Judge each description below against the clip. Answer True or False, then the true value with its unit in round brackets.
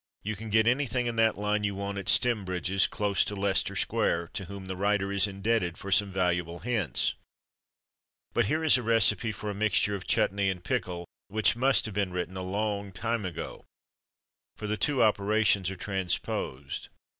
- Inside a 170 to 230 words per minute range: True (180 wpm)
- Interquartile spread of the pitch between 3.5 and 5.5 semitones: False (2.6 semitones)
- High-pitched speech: False (100 Hz)